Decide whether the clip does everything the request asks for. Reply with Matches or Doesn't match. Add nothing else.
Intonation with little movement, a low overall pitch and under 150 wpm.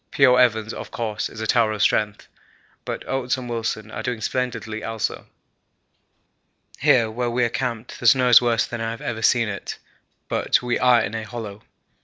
Doesn't match